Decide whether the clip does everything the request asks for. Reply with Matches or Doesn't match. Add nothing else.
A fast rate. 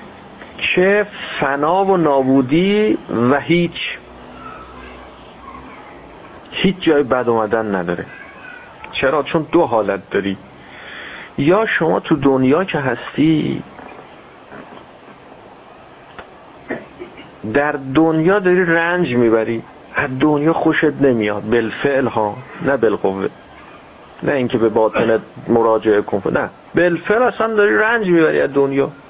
Doesn't match